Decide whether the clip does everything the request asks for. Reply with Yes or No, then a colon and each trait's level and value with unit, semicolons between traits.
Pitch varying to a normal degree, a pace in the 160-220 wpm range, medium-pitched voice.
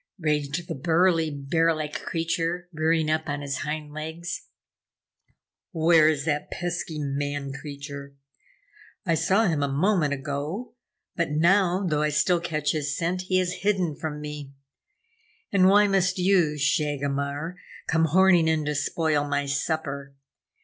No: average, 3.2 semitones; average, 140 wpm; medium, 155 Hz